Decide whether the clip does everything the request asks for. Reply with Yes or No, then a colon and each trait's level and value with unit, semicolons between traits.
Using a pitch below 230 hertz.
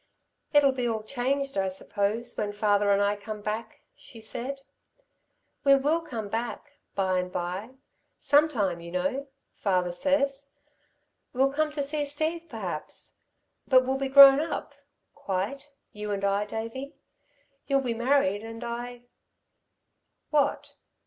No: high, 240 Hz